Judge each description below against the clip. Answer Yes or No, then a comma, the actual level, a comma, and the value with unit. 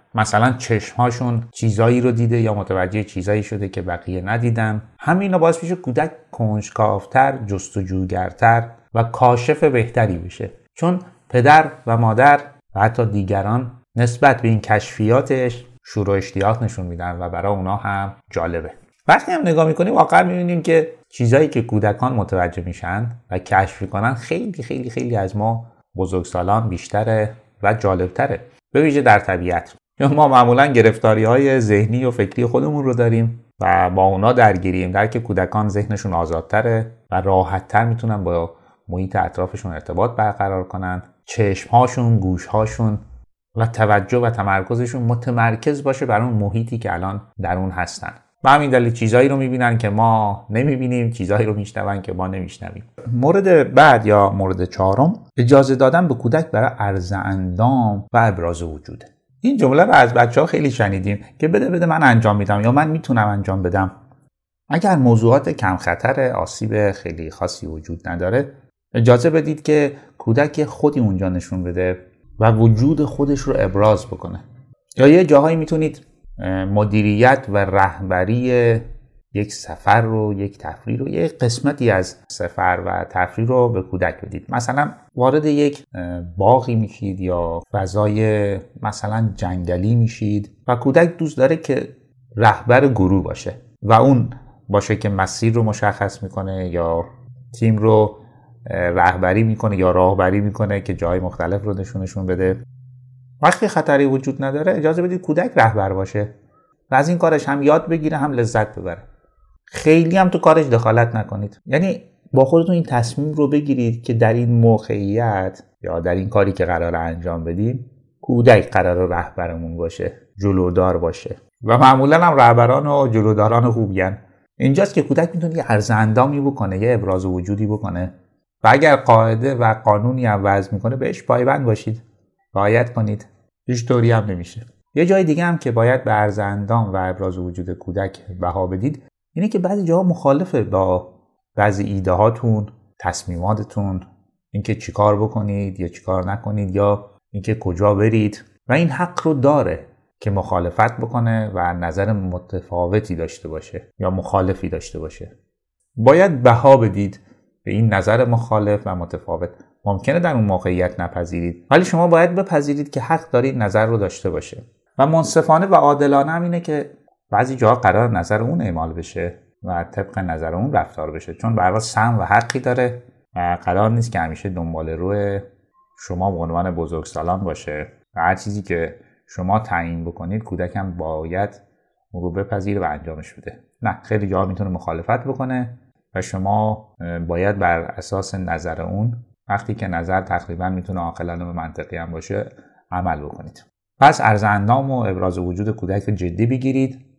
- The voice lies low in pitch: Yes, low, 110 Hz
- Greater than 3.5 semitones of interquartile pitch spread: Yes, average, 4.9 semitones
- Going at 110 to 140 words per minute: No, average, 150 wpm